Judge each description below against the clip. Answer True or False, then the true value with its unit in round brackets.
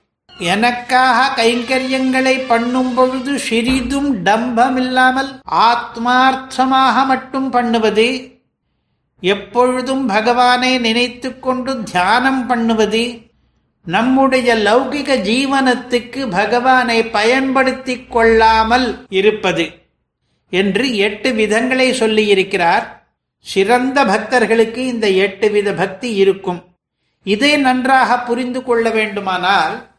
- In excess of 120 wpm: False (75 wpm)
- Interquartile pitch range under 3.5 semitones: True (3.0 semitones)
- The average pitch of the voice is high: True (245 Hz)